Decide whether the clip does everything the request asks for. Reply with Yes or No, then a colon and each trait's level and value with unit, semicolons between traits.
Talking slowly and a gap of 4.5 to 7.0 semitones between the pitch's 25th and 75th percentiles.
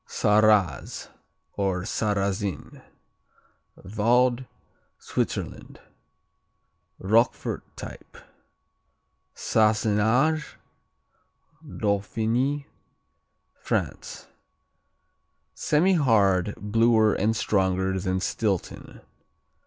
No: slow, 50 wpm; average, 3.1 semitones